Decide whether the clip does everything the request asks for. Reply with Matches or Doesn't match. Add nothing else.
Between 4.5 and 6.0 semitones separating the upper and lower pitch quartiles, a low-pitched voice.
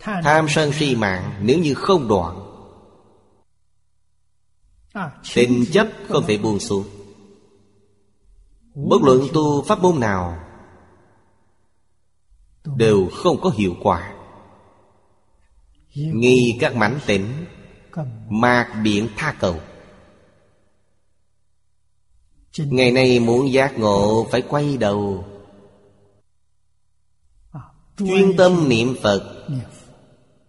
Doesn't match